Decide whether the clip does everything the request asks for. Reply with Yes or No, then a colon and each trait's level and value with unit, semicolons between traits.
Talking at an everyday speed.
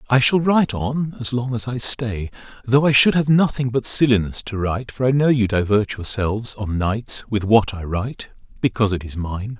No: fast, 215 wpm